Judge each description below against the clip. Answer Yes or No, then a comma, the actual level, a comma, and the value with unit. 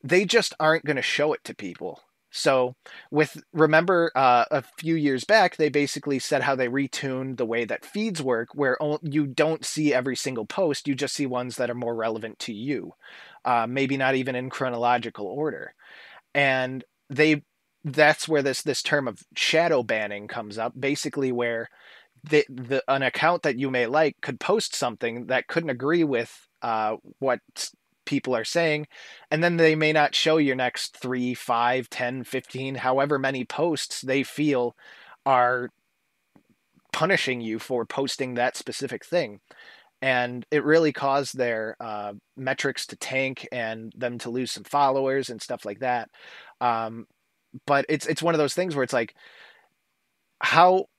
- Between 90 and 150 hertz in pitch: Yes, low, 135 Hz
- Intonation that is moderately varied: Yes, average, 3.4 semitones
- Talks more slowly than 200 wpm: Yes, average, 165 wpm